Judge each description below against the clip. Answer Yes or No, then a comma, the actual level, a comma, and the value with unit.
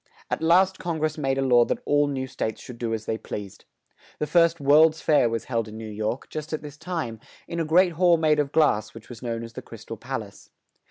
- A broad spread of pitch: Yes, wide, 5.7 semitones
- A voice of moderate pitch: Yes, medium, 145 Hz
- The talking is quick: Yes, fast, 250 wpm